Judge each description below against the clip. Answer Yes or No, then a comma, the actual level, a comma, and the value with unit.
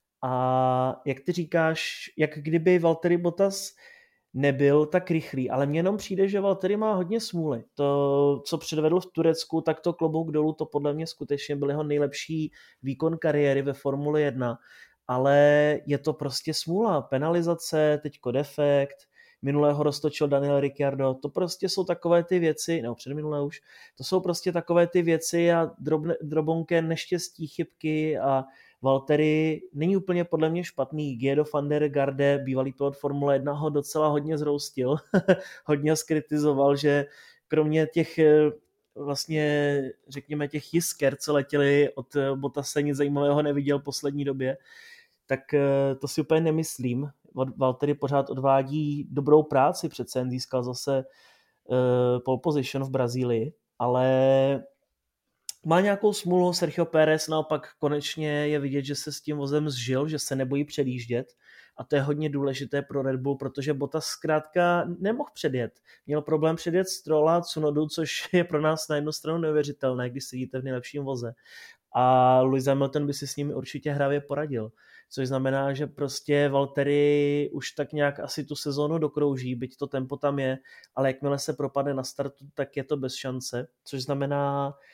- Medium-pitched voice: Yes, medium, 145 Hz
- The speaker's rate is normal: Yes, average, 160 wpm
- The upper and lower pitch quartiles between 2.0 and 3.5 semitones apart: Yes, narrow, 2.4 semitones